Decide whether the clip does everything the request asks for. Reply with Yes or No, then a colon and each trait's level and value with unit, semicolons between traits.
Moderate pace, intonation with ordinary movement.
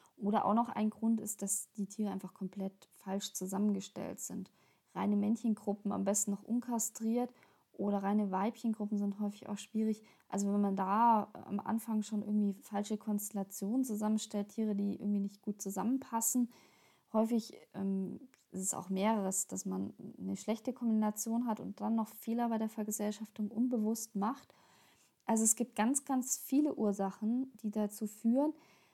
No: average, 155 wpm; narrow, 2.1 semitones